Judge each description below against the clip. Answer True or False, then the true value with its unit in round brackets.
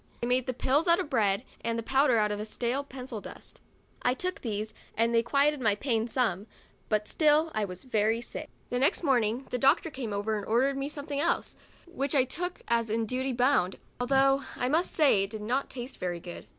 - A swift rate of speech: True (210 wpm)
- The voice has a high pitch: True (250 Hz)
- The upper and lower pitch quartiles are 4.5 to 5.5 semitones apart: False (4.1 semitones)